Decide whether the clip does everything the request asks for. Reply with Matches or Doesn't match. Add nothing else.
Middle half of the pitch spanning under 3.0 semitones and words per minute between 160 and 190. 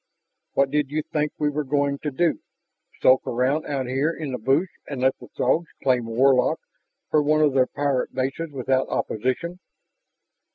Matches